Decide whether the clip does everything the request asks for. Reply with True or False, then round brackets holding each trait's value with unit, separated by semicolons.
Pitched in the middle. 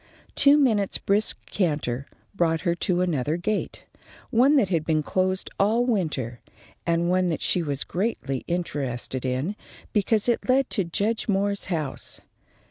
True (180 Hz)